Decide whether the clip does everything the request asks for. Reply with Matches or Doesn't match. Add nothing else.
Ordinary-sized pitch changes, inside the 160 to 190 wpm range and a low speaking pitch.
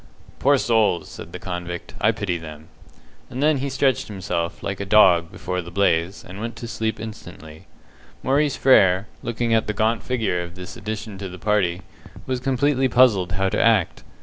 Matches